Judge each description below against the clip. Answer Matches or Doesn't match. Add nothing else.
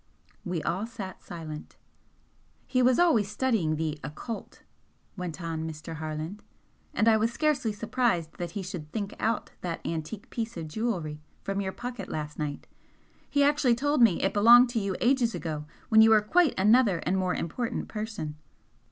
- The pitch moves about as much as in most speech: Doesn't match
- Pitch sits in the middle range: Doesn't match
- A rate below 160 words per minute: Doesn't match